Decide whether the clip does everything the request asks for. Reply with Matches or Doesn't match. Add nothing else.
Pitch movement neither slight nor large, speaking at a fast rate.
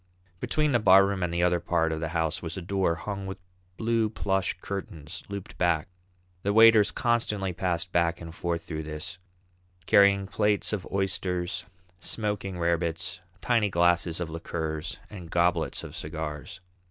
Doesn't match